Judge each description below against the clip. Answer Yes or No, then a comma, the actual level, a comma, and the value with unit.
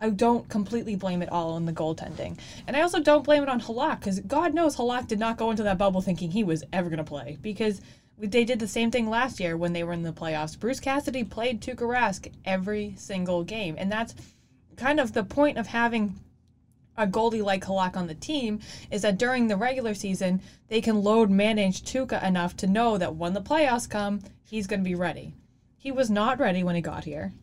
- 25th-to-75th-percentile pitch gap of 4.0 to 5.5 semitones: Yes, average, 4.5 semitones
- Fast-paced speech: Yes, fast, 225 wpm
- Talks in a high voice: Yes, high, 210 Hz